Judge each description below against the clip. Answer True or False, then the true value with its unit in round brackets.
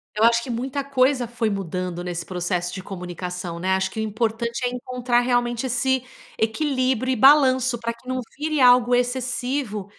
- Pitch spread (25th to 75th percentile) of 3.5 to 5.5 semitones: True (4.4 semitones)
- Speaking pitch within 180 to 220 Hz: False (240 Hz)